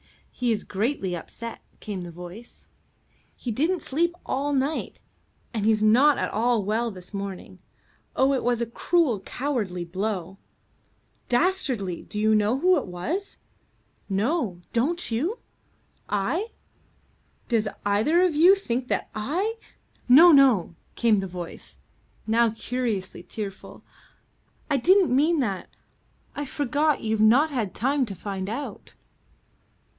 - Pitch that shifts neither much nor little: No, wide, 6.3 semitones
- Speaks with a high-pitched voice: Yes, high, 235 Hz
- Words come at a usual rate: No, slow, 130 wpm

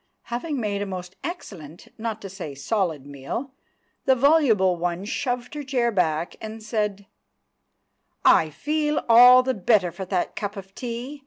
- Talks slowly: No, average, 155 wpm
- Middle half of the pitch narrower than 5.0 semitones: No, wide, 5.5 semitones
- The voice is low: No, high, 210 Hz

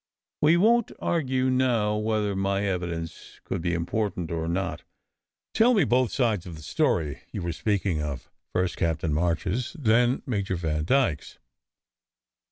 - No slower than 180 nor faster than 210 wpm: No, average, 155 wpm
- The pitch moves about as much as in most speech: No, wide, 7.0 semitones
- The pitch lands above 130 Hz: No, low, 100 Hz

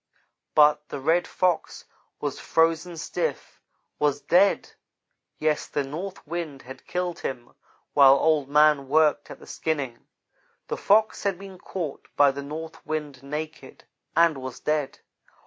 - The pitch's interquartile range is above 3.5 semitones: No, average, 3.1 semitones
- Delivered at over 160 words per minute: No, average, 140 wpm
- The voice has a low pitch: No, medium, 155 Hz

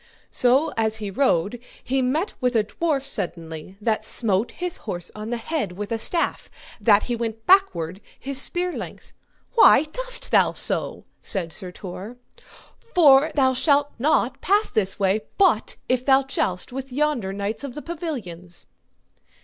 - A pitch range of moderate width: No, wide, 6.5 semitones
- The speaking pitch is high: Yes, high, 245 Hz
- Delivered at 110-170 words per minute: Yes, average, 155 wpm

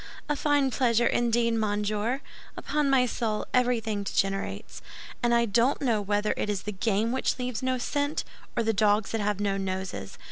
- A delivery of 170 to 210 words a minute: Yes, average, 175 wpm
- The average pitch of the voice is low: No, high, 225 Hz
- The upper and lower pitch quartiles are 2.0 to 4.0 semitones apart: Yes, average, 3.4 semitones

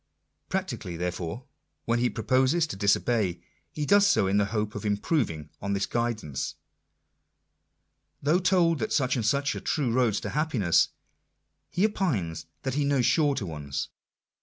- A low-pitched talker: Yes, low, 120 Hz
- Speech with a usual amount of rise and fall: No, wide, 6.9 semitones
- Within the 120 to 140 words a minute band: No, average, 155 wpm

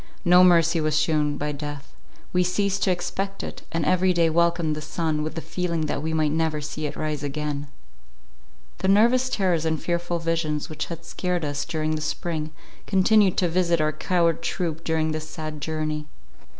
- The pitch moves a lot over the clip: No, narrow, 2.5 semitones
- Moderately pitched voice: Yes, medium, 160 Hz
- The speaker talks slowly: No, average, 185 wpm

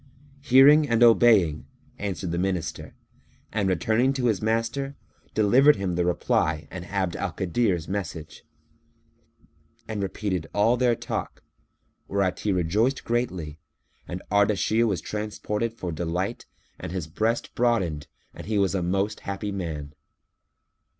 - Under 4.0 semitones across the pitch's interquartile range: No, average, 4.5 semitones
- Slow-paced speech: Yes, slow, 130 wpm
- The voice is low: Yes, low, 100 Hz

